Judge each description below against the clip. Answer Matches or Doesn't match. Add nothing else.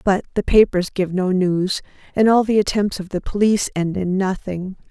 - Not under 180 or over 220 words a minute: Matches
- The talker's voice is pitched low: Doesn't match